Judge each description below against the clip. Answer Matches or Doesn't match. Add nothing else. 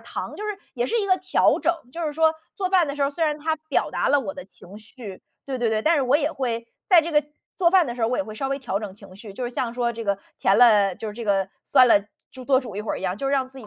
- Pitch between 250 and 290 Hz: Matches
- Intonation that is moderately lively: Doesn't match